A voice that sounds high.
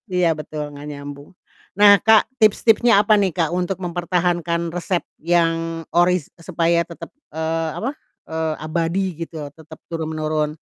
No: medium, 170 Hz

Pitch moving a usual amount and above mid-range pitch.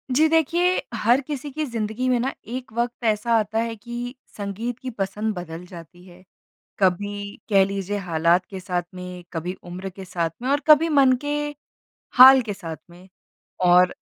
No: wide, 5.8 semitones; high, 210 Hz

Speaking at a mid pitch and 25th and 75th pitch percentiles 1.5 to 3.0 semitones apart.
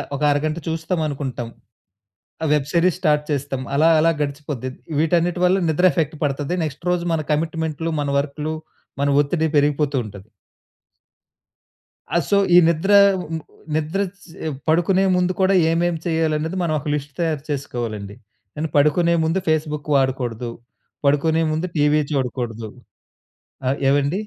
Yes: medium, 150 Hz; average, 2.7 semitones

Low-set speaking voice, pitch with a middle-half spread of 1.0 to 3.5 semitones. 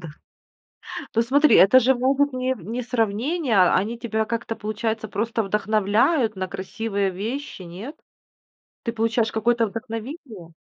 No: high, 225 Hz; average, 3.1 semitones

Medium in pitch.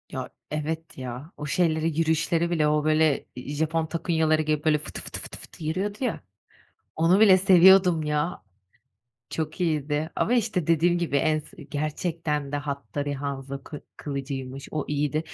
Yes: medium, 155 Hz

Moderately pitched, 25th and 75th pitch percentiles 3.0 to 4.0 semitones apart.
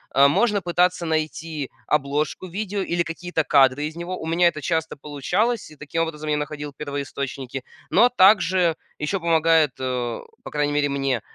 Yes: medium, 155 Hz; average, 3.5 semitones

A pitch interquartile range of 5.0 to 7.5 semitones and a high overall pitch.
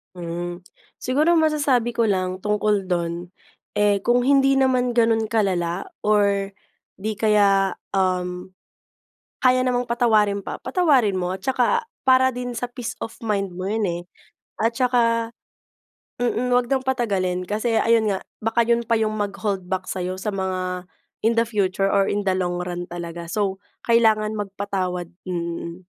No: average, 4.3 semitones; high, 210 Hz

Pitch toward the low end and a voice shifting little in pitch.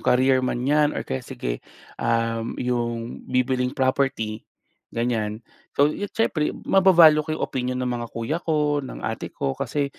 No: low, 125 Hz; average, 4.1 semitones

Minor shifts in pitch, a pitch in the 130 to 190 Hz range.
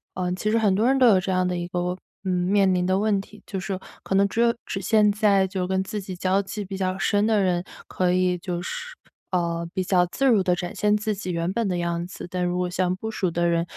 Yes: narrow, 2.3 semitones; medium, 185 Hz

